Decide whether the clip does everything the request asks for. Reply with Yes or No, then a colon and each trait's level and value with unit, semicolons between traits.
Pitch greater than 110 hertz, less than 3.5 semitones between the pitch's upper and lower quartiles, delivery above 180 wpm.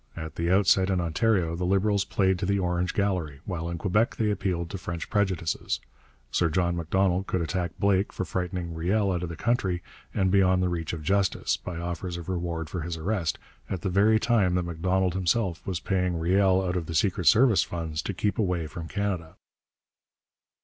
No: very low, 90 Hz; narrow, 2.4 semitones; average, 195 wpm